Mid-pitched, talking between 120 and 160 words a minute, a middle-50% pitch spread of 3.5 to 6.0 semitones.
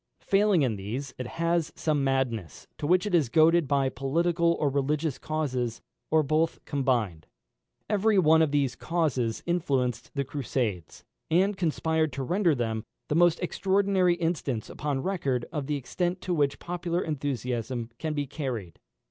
Yes: medium, 150 Hz; average, 155 wpm; average, 4.8 semitones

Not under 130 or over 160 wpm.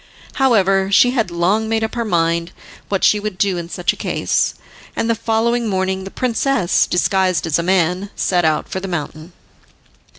No: average, 185 wpm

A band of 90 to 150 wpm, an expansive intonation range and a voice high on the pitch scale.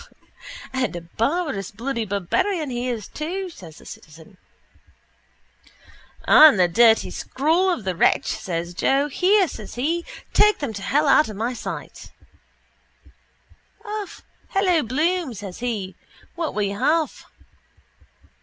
Yes: slow, 135 wpm; wide, 8.5 semitones; very high, 250 Hz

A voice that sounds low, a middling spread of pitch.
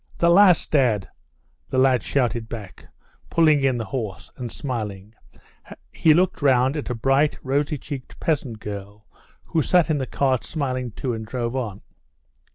Yes: low, 130 Hz; average, 4.4 semitones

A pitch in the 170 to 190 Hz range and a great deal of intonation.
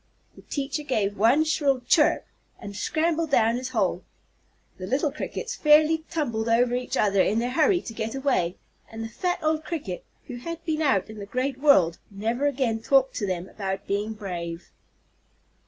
No: high, 245 Hz; wide, 6.5 semitones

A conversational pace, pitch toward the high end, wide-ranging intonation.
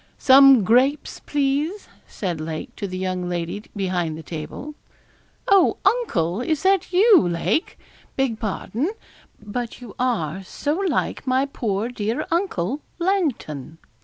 No: slow, 130 wpm; high, 235 Hz; wide, 8.4 semitones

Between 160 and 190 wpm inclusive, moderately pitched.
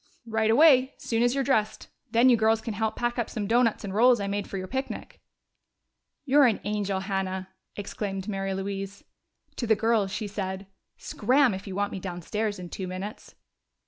No: average, 185 wpm; high, 210 Hz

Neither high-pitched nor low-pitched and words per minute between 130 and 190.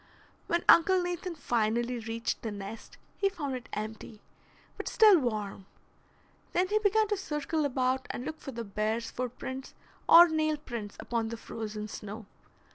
No: very high, 255 Hz; average, 155 wpm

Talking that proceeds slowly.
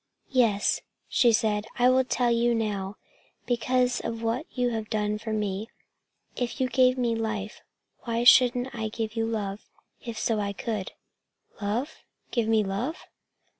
No: average, 155 wpm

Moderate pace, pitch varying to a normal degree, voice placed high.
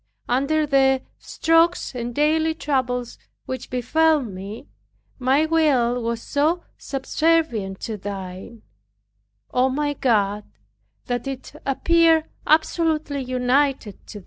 No: slow, 110 wpm; average, 4.7 semitones; very high, 265 Hz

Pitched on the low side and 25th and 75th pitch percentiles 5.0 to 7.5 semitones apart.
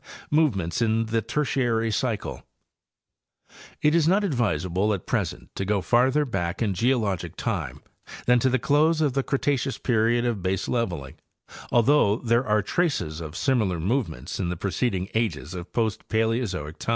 Yes: low, 115 Hz; wide, 5.5 semitones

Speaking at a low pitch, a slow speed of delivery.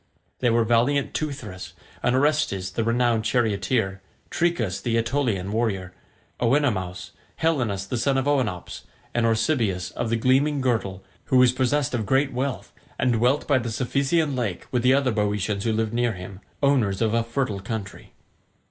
No: low, 120 Hz; average, 160 wpm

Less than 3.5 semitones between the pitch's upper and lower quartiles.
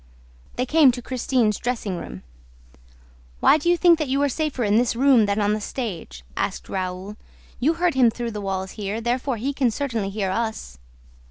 No: average, 4.7 semitones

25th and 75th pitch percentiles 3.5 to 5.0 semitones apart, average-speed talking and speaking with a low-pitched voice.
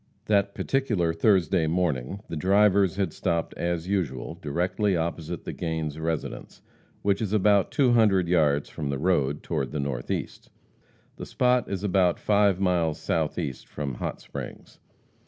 Yes: average, 4.2 semitones; average, 145 wpm; very low, 90 Hz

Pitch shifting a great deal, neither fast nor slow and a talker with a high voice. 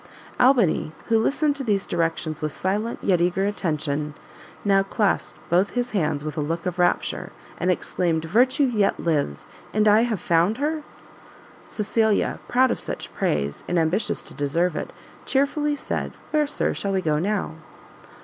Yes: wide, 5.9 semitones; average, 160 wpm; high, 195 Hz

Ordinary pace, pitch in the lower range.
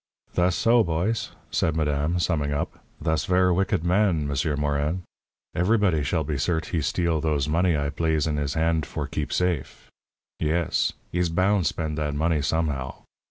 Yes: average, 160 wpm; very low, 80 Hz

